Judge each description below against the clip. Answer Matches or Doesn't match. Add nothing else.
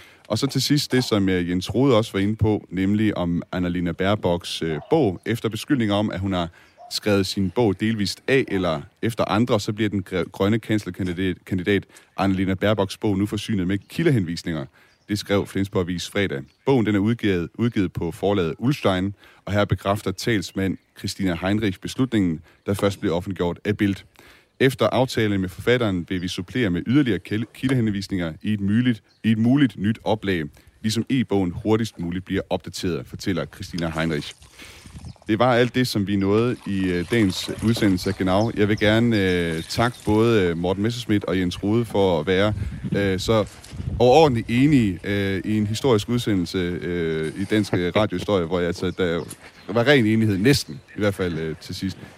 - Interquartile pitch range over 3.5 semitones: Doesn't match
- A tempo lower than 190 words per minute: Matches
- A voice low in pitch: Matches